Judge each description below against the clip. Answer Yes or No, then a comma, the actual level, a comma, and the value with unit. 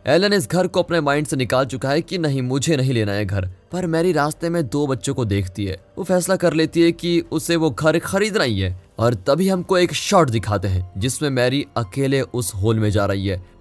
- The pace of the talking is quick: Yes, fast, 240 wpm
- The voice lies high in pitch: No, medium, 140 Hz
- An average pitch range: No, wide, 7.6 semitones